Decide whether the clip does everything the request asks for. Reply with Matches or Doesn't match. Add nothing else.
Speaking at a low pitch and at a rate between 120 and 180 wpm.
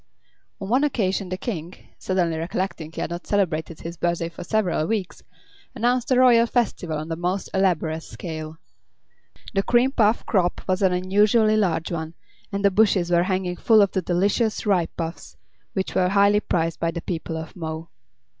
Doesn't match